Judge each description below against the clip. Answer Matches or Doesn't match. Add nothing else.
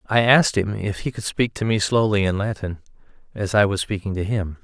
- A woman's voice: Doesn't match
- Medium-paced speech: Doesn't match